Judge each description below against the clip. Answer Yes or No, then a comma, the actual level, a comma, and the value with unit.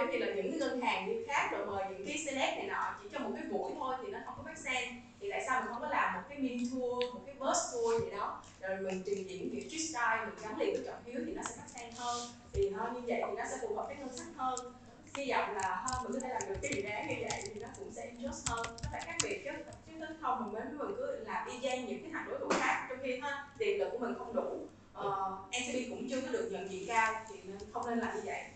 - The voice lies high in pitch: Yes, very high, 250 Hz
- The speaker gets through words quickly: Yes, fast, 290 wpm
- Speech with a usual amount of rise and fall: Yes, average, 5.0 semitones